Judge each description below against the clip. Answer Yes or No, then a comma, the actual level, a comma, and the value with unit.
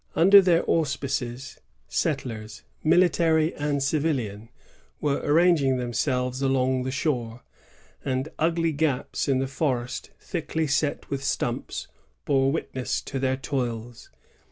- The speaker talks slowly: Yes, slow, 120 wpm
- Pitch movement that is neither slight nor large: Yes, average, 3.6 semitones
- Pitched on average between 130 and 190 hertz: Yes, low, 135 Hz